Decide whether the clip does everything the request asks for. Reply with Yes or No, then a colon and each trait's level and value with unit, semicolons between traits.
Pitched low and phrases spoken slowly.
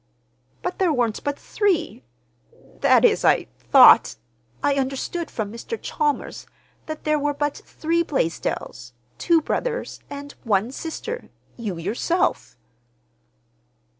No: very high, 280 Hz; slow, 105 wpm